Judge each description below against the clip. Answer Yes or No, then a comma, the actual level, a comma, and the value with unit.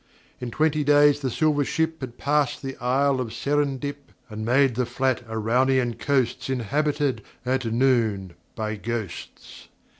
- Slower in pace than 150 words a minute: Yes, average, 140 wpm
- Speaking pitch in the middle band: No, low, 130 Hz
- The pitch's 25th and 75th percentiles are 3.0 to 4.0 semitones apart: Yes, average, 3.4 semitones